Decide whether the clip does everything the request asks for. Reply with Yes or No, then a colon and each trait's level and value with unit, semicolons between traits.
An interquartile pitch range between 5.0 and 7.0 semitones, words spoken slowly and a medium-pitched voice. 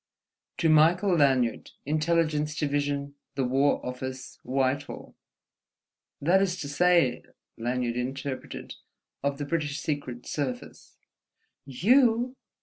No: average, 3.9 semitones; slow, 100 wpm; medium, 145 Hz